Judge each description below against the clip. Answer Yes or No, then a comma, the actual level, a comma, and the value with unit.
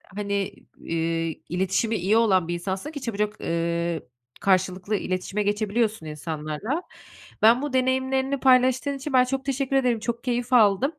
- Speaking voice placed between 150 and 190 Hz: No, high, 215 Hz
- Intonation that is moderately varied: No, wide, 5.8 semitones